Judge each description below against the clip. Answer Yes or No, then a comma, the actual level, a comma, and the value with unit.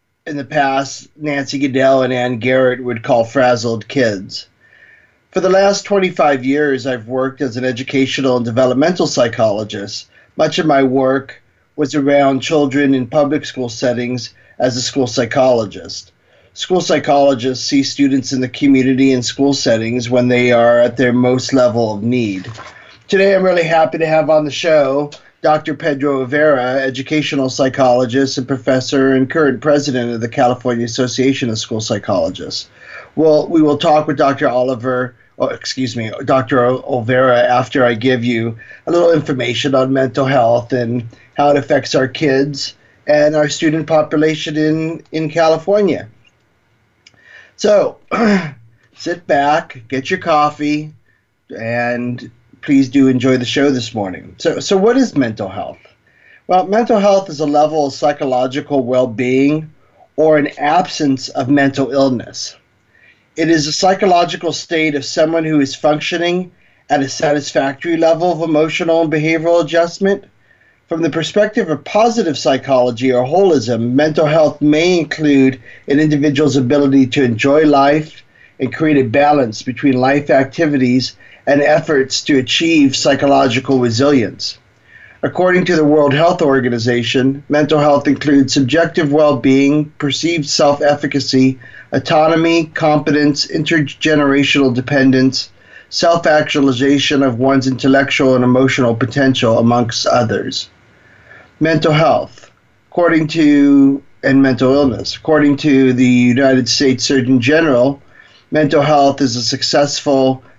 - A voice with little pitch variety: No, average, 3.2 semitones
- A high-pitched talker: No, medium, 140 Hz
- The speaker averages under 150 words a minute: Yes, slow, 135 wpm